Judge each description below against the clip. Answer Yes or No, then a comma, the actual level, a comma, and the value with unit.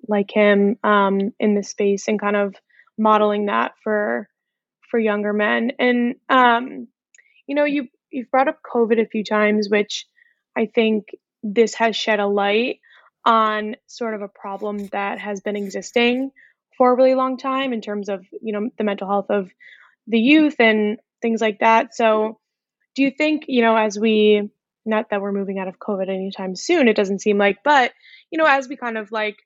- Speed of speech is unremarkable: Yes, average, 190 wpm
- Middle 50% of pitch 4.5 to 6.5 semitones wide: No, average, 3.2 semitones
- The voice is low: No, high, 220 Hz